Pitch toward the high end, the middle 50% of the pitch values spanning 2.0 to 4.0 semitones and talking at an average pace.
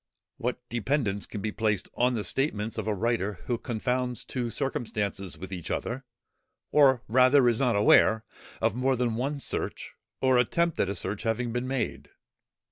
No: low, 120 Hz; average, 3.2 semitones; average, 170 wpm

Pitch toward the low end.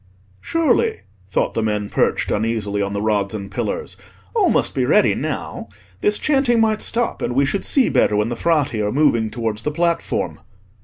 Yes: low, 115 Hz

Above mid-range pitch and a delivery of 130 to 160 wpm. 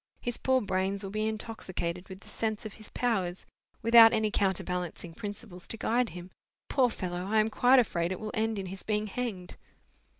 No: high, 210 Hz; average, 190 wpm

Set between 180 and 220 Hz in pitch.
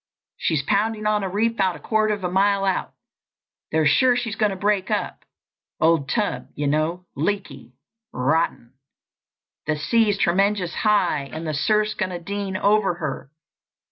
Yes: high, 190 Hz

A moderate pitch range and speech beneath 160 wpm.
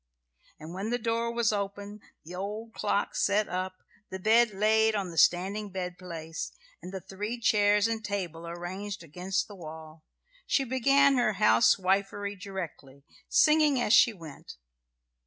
Yes: average, 3.5 semitones; average, 150 wpm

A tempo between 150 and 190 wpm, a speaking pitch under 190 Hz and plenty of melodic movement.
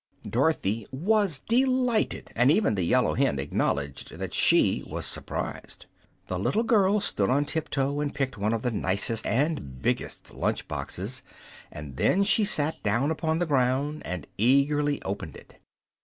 Yes: average, 155 wpm; medium, 140 Hz; wide, 7.6 semitones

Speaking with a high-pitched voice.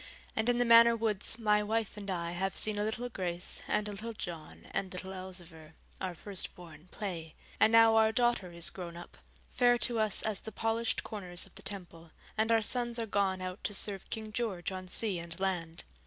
Yes: high, 200 Hz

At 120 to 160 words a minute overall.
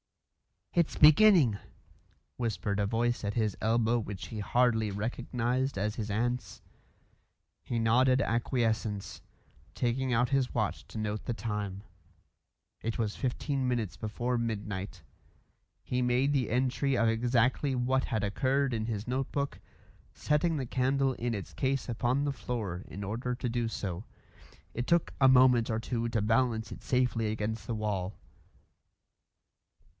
Yes: average, 140 wpm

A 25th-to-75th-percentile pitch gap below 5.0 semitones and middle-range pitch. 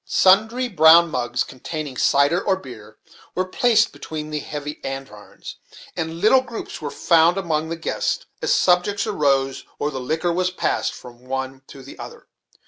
No: average, 5.3 semitones; medium, 160 Hz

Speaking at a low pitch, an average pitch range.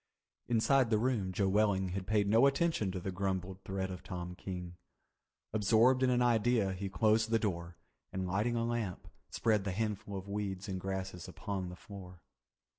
Yes: low, 100 Hz; average, 3.0 semitones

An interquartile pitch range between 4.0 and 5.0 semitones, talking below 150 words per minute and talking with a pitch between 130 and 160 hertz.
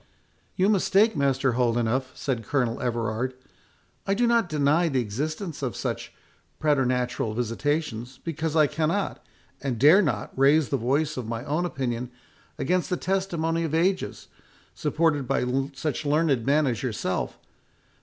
Yes: average, 4.6 semitones; average, 140 wpm; medium, 140 Hz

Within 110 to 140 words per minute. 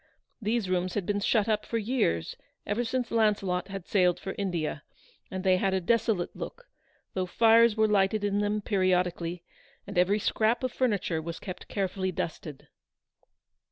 No: average, 160 wpm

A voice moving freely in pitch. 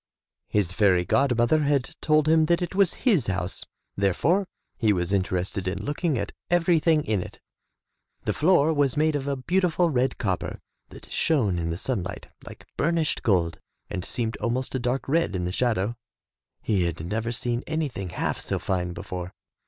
Yes: wide, 8.5 semitones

